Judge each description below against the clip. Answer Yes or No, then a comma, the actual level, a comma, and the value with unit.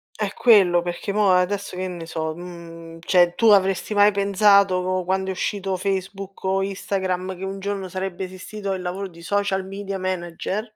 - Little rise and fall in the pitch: Yes, narrow, 1.6 semitones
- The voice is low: No, high, 190 Hz